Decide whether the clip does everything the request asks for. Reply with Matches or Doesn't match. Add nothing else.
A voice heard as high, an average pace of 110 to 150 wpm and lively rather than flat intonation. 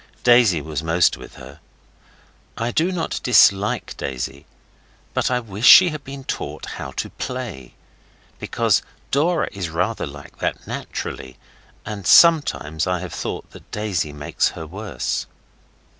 Doesn't match